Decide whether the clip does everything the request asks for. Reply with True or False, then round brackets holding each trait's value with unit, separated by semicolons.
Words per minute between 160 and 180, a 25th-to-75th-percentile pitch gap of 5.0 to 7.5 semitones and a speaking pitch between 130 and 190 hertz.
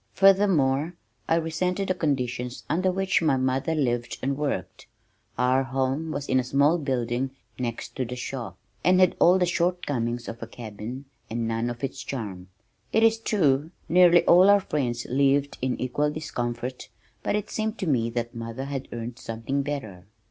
True (170 wpm; 5.5 semitones; 135 Hz)